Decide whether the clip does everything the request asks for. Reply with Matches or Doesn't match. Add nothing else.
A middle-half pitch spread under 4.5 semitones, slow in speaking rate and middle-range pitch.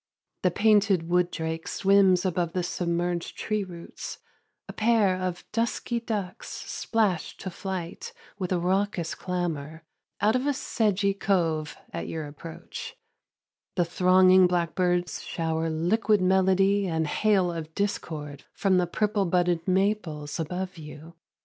Matches